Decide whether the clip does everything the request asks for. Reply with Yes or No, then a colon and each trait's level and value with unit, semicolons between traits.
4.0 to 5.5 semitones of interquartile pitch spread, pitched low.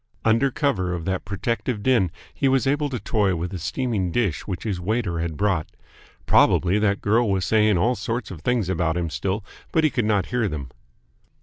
Yes: average, 5.0 semitones; low, 105 Hz